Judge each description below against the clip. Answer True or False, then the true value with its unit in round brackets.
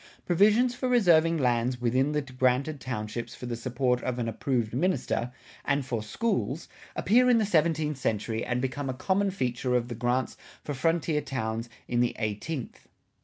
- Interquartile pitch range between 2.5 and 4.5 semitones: False (5.3 semitones)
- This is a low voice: True (130 Hz)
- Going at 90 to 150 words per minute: False (170 wpm)